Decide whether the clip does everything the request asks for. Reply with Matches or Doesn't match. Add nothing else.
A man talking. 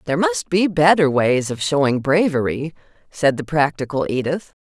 Doesn't match